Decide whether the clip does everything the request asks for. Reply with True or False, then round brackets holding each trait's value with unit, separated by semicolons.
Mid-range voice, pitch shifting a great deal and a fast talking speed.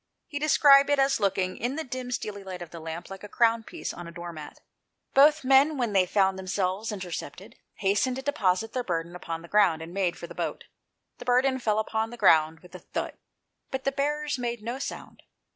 False (210 Hz; 6.2 semitones; 220 wpm)